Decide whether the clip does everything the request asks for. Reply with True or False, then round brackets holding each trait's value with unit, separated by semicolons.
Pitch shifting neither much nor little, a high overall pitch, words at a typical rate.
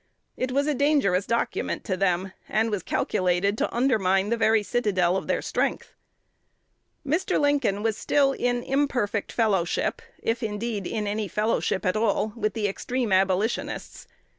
True (3.9 semitones; 215 Hz; 150 wpm)